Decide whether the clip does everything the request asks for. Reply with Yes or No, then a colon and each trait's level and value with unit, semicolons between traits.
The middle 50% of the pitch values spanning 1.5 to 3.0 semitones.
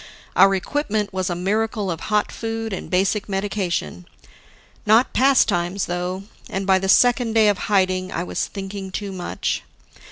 Yes: narrow, 2.5 semitones